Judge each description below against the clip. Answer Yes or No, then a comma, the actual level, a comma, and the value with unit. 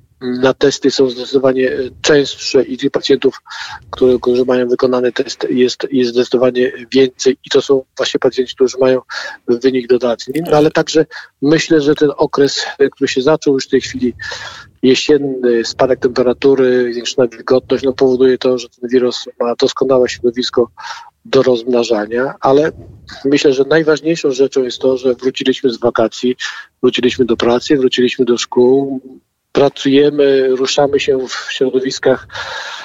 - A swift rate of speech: No, average, 140 wpm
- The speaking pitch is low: Yes, low, 130 Hz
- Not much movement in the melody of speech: Yes, narrow, 1.6 semitones